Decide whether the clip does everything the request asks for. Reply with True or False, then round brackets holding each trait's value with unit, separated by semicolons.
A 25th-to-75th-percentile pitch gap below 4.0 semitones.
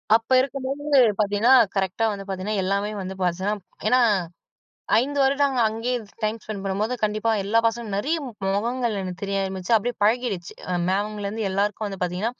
True (3.2 semitones)